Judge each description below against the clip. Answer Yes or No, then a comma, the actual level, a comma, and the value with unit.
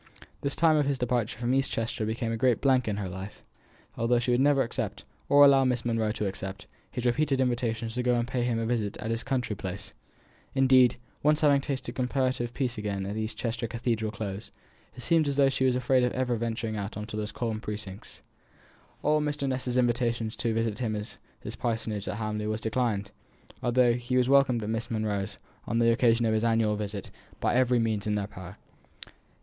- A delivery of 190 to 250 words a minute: Yes, fast, 205 wpm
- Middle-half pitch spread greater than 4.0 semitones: No, average, 2.8 semitones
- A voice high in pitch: No, low, 115 Hz